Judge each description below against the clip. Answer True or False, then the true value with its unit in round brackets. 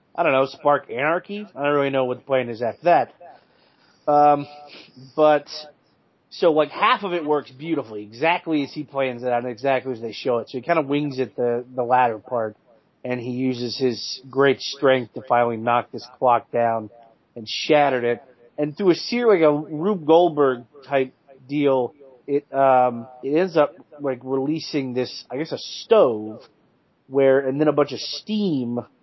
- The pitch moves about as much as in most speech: True (3.2 semitones)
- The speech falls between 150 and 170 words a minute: False (185 wpm)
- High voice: False (135 Hz)